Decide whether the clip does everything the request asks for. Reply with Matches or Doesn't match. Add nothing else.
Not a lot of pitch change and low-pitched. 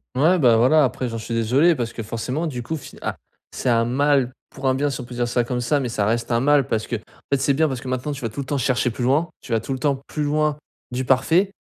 Doesn't match